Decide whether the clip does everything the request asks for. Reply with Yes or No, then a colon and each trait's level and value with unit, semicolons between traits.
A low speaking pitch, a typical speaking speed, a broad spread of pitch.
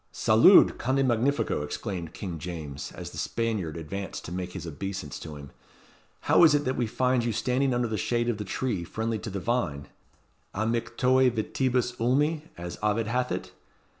Yes: low, 110 Hz; average, 175 wpm; wide, 5.9 semitones